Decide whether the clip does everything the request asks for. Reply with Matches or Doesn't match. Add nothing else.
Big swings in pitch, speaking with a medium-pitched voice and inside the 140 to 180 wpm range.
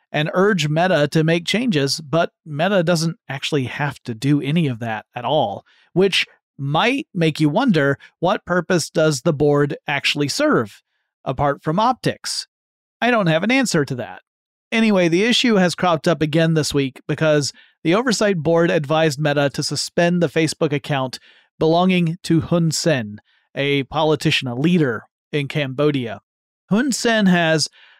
Doesn't match